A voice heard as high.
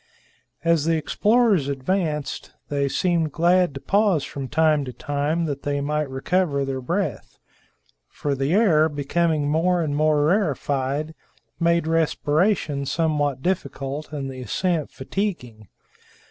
No: medium, 150 Hz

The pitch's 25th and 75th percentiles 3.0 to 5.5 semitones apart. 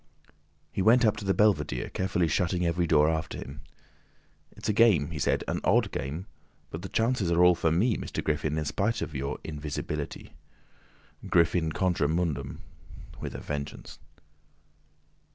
Yes: average, 3.9 semitones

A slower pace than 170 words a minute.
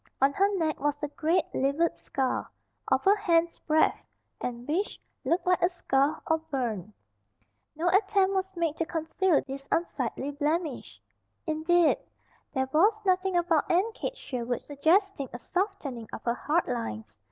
Yes: average, 155 wpm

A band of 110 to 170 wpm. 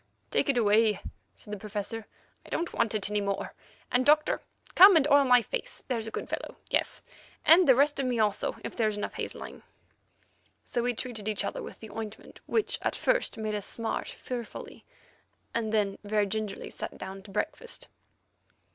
No: average, 185 wpm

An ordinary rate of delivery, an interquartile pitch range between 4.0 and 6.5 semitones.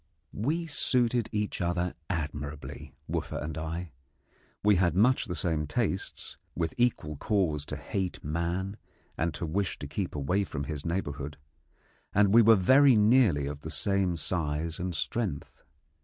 Yes: average, 150 wpm; average, 5.2 semitones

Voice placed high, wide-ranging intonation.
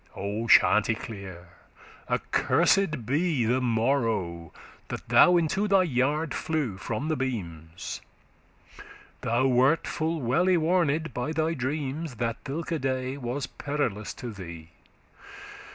No: low, 130 Hz; wide, 5.8 semitones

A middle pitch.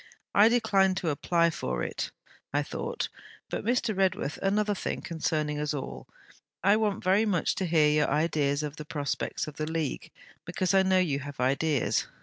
Yes: medium, 165 Hz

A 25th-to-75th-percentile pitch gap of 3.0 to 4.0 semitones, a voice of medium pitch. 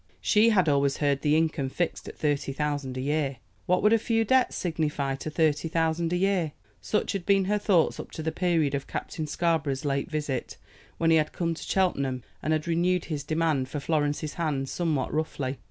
Yes: average, 3.3 semitones; medium, 155 Hz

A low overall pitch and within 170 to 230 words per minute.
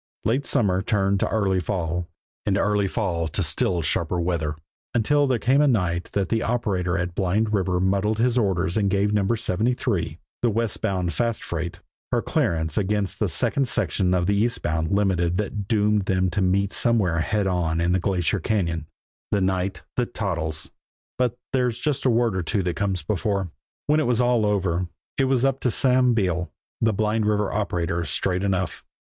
Yes: low, 100 Hz; average, 180 wpm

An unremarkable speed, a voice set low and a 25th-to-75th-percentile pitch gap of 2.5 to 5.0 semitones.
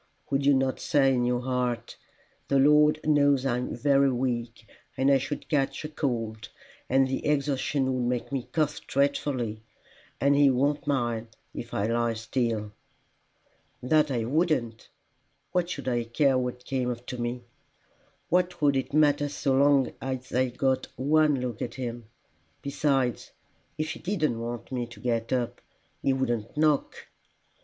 Yes: average, 155 wpm; low, 130 Hz; average, 2.9 semitones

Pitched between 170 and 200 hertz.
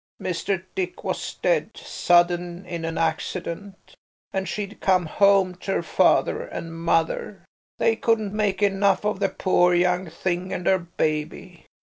Yes: medium, 185 Hz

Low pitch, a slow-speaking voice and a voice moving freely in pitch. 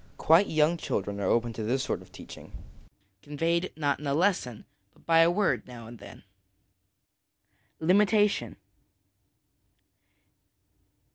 No: medium, 155 Hz; slow, 125 wpm; wide, 6.3 semitones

